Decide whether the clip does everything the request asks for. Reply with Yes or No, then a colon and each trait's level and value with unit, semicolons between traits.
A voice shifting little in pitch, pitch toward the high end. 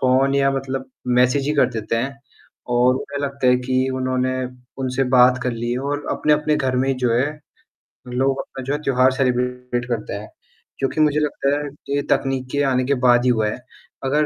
No: narrow, 1.7 semitones; low, 130 Hz